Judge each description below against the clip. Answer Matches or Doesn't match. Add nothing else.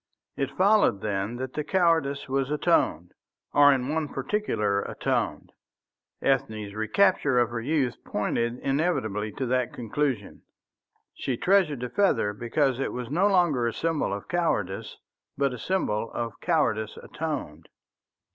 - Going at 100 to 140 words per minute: Matches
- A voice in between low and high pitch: Doesn't match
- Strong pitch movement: Matches